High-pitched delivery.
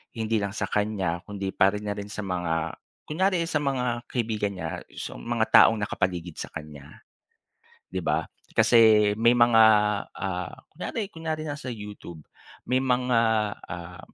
No: low, 105 Hz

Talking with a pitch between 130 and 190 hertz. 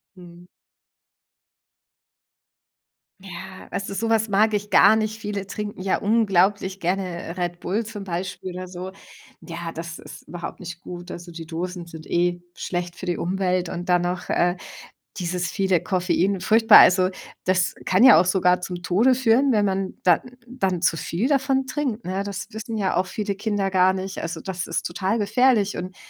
Yes: medium, 185 Hz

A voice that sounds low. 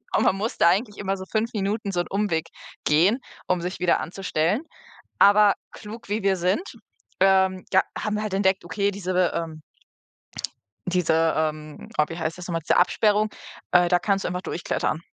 No: high, 190 Hz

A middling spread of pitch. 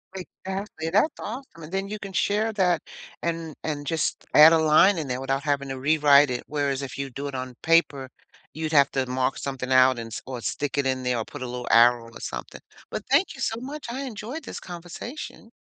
No: wide, 6.3 semitones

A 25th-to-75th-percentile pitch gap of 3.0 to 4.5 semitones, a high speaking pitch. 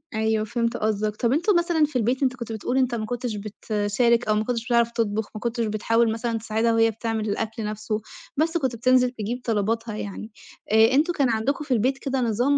No: narrow, 2.6 semitones; high, 230 Hz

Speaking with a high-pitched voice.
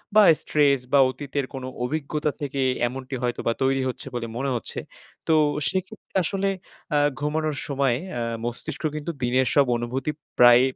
No: medium, 140 Hz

